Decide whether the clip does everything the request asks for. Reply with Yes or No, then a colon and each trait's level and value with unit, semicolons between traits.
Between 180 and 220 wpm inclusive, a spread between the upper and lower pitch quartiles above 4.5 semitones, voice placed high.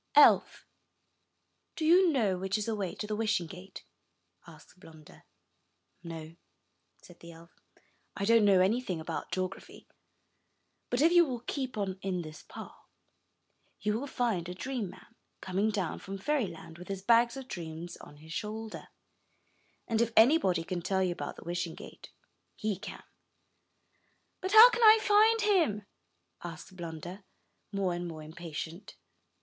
No: average, 155 wpm; average, 5.2 semitones; high, 195 Hz